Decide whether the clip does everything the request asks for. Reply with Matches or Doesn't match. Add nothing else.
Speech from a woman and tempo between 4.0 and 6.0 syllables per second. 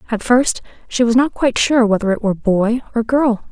Matches